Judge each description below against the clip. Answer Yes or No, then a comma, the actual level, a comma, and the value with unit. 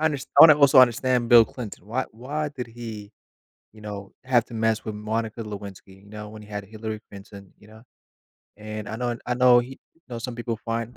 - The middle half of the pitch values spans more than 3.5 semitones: No, narrow, 2.6 semitones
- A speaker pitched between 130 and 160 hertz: No, low, 115 Hz